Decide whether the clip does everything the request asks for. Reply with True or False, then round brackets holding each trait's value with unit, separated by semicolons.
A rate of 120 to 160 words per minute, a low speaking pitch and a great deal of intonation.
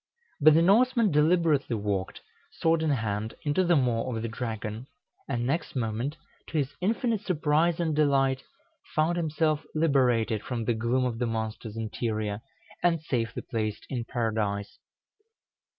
True (145 wpm; 130 Hz; 5.9 semitones)